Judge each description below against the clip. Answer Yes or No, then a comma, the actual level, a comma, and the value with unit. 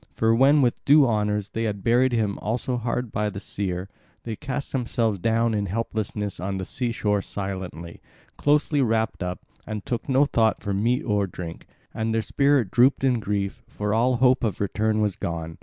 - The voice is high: No, low, 110 Hz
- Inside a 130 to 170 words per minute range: No, average, 190 wpm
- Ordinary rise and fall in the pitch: Yes, average, 3.5 semitones